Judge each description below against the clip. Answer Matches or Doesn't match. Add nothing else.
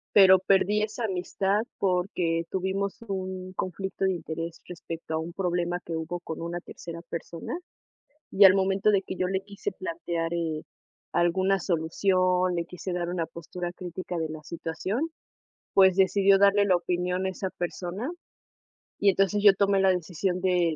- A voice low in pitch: Doesn't match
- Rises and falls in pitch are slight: Matches